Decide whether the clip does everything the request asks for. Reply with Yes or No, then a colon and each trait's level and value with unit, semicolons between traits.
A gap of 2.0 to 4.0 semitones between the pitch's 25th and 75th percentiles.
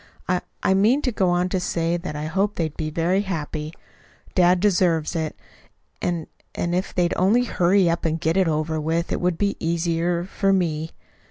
Yes: narrow, 2.6 semitones